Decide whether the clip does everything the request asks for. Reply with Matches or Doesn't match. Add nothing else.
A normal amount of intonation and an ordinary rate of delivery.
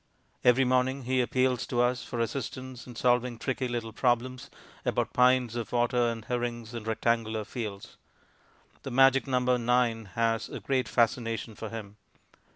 Doesn't match